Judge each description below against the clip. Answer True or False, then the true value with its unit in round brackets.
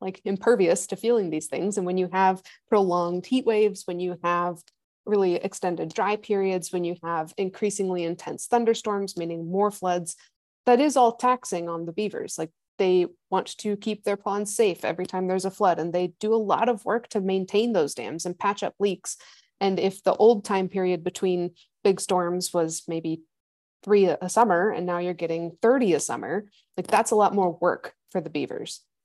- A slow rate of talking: False (195 wpm)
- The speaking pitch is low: False (190 Hz)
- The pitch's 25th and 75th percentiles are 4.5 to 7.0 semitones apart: False (2.9 semitones)